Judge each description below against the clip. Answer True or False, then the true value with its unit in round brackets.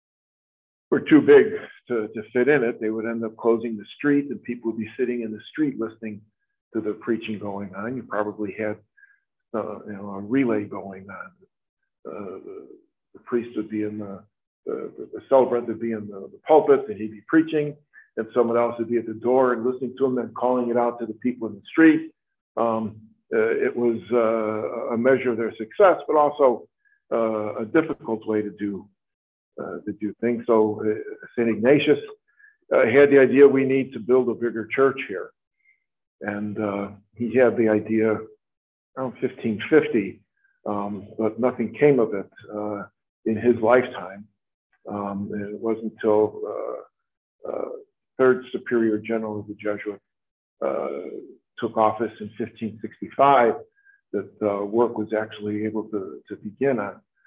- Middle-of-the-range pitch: False (115 Hz)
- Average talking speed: True (175 wpm)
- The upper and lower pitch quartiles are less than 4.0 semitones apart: False (5.0 semitones)